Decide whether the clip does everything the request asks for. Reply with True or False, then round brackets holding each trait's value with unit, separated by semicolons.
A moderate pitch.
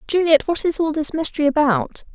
False (305 Hz)